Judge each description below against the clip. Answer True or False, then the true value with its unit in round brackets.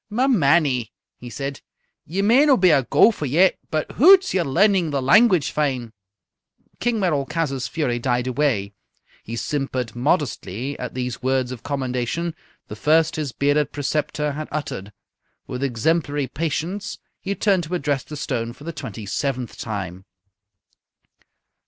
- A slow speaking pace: False (145 wpm)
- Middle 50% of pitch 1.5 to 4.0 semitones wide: False (5.0 semitones)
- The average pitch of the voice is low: False (145 Hz)